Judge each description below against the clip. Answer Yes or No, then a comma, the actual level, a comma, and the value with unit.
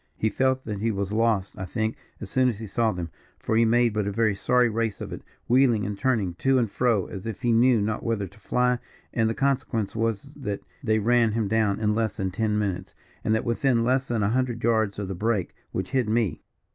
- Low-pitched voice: Yes, low, 110 Hz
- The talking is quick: Yes, fast, 235 wpm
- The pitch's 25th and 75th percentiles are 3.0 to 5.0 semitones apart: No, narrow, 2.6 semitones